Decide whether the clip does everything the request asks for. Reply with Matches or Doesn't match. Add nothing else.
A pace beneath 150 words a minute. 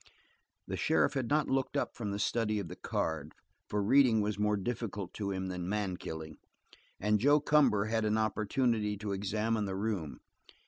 Doesn't match